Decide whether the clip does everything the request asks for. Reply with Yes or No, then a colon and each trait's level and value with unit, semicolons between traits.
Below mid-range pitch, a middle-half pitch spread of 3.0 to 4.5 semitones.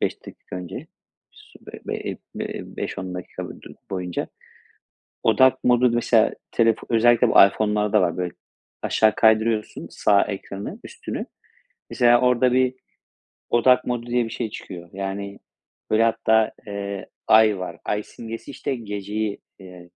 Yes: low, 110 Hz; average, 3.3 semitones